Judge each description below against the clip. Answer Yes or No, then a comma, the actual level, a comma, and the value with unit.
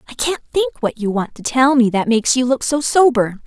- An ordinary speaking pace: No, fast, 260 wpm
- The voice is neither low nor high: No, very high, 255 Hz